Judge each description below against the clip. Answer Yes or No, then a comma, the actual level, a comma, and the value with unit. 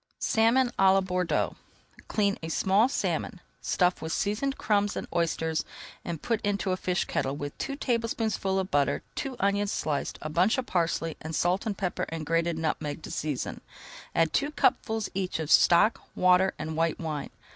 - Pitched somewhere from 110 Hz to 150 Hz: No, medium, 185 Hz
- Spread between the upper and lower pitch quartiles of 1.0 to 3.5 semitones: No, average, 4.3 semitones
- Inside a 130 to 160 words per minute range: No, average, 170 wpm